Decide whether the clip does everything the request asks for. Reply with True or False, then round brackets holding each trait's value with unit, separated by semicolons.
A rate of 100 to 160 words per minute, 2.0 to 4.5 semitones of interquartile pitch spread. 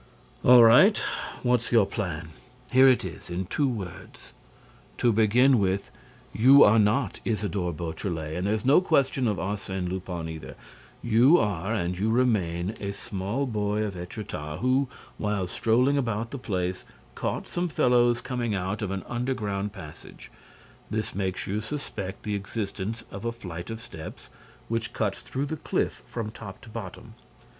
True (155 wpm; 4.2 semitones)